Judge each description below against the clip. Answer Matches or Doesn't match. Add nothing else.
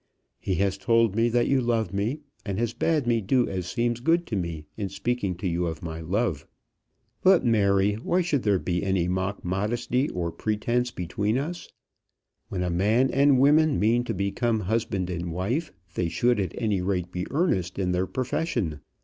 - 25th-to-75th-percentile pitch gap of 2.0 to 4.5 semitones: Doesn't match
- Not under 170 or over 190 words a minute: Matches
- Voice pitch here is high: Doesn't match